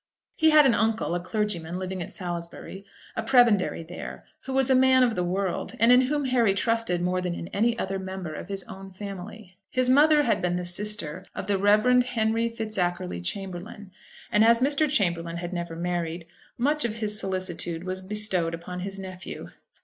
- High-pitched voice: Yes, high, 195 Hz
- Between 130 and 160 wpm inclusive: No, average, 190 wpm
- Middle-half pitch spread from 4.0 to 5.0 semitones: Yes, average, 4.5 semitones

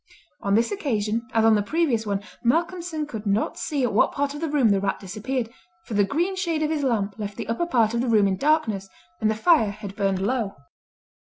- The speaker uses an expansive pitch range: Yes, wide, 6.4 semitones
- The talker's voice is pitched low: No, high, 230 Hz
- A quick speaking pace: Yes, fast, 230 wpm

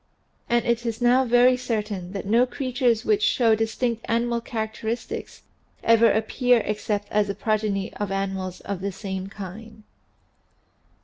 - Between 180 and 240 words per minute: No, average, 140 wpm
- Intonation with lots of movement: No, average, 2.9 semitones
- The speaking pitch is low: No, high, 225 Hz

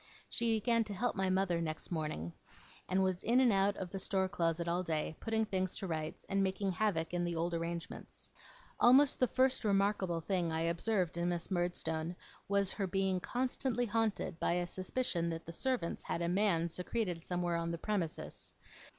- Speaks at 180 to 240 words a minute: Yes, average, 185 wpm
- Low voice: No, medium, 185 Hz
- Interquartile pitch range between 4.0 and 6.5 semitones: No, average, 3.4 semitones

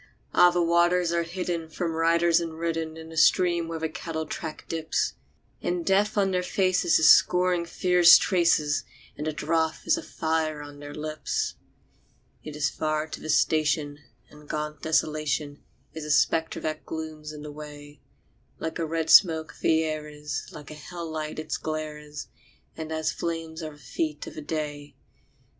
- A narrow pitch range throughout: Yes, narrow, 1.7 semitones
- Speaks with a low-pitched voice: No, medium, 160 Hz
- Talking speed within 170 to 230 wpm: Yes, average, 175 wpm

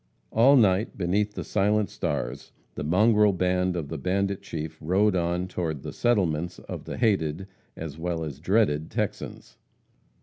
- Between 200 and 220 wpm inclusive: No, average, 155 wpm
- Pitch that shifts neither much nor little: Yes, average, 4.2 semitones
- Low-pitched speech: Yes, very low, 90 Hz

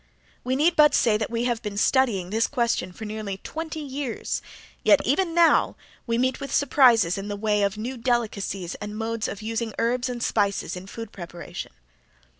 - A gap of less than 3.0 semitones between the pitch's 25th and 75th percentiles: No, average, 3.9 semitones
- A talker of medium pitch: No, high, 230 Hz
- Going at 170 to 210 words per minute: Yes, average, 185 wpm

